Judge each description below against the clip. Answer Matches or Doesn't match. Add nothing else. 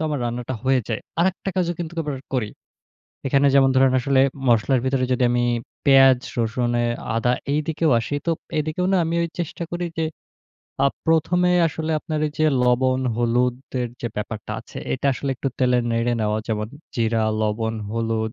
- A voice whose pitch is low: Matches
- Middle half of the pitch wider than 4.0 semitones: Matches